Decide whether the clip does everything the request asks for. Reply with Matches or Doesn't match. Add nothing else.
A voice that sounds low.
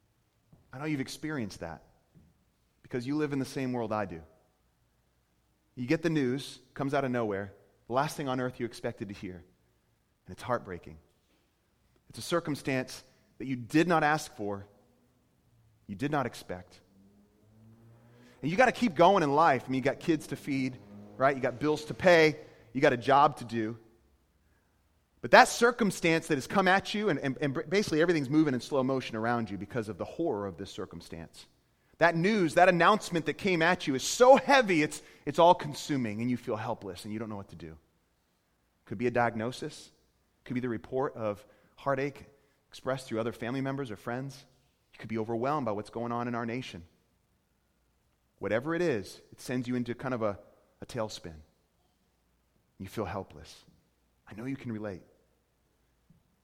Matches